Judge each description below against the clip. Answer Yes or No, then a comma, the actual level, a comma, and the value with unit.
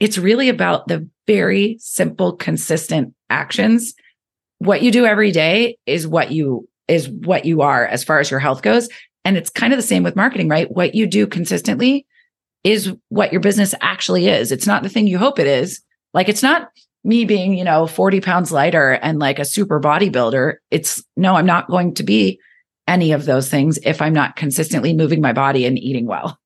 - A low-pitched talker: No, medium, 185 Hz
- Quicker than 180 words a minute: Yes, average, 200 wpm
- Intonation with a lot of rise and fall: Yes, wide, 6.0 semitones